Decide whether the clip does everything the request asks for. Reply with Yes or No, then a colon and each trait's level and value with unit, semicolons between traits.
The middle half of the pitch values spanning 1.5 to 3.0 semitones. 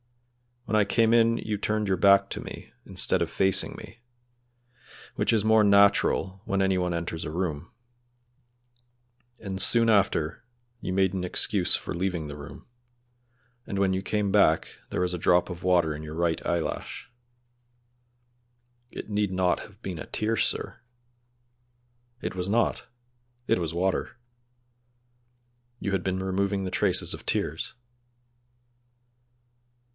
Yes: narrow, 2.5 semitones